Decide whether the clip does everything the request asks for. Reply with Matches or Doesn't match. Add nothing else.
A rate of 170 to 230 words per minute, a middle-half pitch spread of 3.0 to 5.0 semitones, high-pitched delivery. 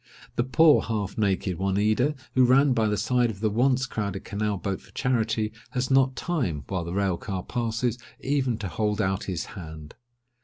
Doesn't match